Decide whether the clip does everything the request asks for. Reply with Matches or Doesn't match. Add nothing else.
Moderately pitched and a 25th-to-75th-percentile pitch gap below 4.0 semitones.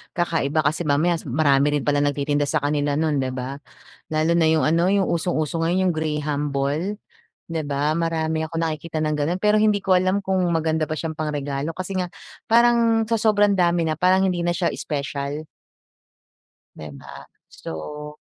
Matches